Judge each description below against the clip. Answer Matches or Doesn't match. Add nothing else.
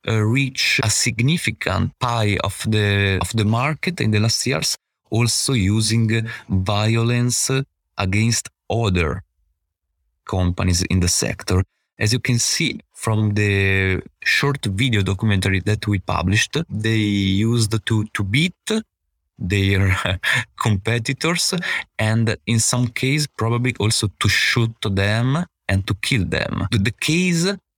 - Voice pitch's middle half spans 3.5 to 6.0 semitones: Matches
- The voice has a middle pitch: Doesn't match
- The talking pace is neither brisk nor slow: Doesn't match